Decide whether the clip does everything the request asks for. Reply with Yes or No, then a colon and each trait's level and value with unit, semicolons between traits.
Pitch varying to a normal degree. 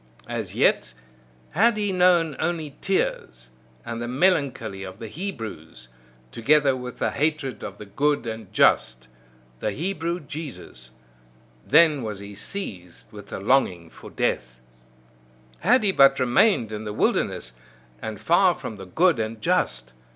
No: wide, 8.5 semitones